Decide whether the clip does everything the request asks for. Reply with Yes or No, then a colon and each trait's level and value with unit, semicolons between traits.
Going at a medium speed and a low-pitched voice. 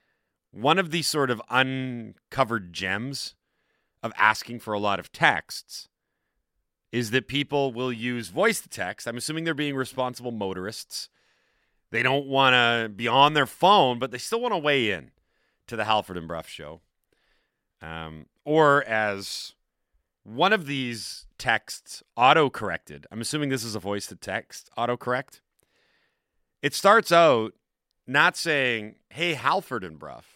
Yes: average, 150 wpm; low, 120 Hz